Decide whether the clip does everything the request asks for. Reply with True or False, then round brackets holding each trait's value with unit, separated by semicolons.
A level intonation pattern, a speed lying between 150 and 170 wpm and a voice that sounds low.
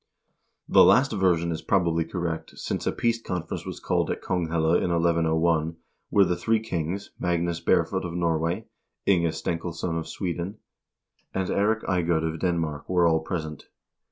True (1.9 semitones; 155 wpm; 85 Hz)